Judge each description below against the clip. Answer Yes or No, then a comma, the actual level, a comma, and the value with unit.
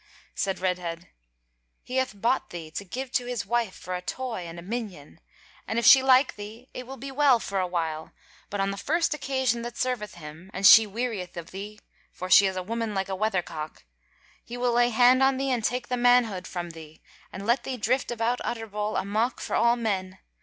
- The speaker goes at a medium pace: No, fast, 215 wpm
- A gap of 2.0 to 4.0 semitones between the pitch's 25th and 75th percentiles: No, average, 4.9 semitones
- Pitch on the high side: Yes, high, 220 Hz